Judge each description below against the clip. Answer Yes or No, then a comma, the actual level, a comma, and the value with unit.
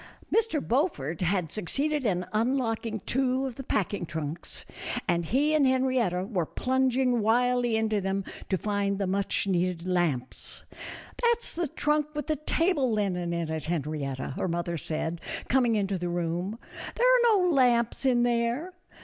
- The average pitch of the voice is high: Yes, high, 220 Hz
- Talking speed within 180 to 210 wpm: No, average, 155 wpm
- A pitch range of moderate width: No, wide, 6.9 semitones